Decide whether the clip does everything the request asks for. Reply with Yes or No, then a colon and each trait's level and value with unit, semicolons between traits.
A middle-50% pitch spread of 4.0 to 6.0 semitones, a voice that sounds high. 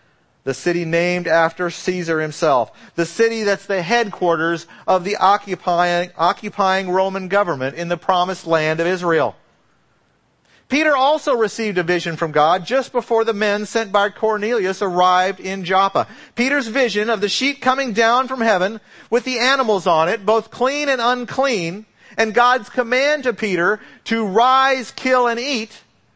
Yes: average, 5.3 semitones; high, 205 Hz